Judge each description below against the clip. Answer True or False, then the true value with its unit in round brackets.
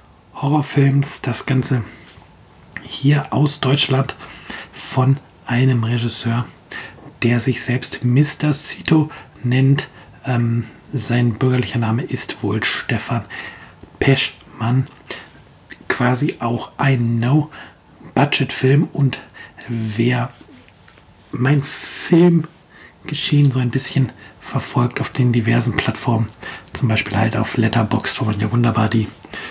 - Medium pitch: False (125 Hz)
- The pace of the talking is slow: True (100 wpm)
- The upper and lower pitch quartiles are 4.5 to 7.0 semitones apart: False (2.8 semitones)